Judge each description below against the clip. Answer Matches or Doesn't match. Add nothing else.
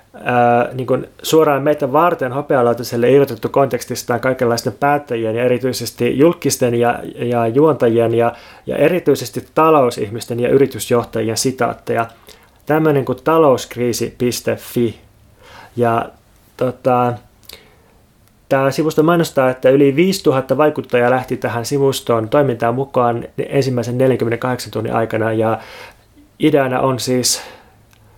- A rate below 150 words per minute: Matches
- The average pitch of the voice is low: Matches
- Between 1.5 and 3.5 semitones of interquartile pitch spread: Matches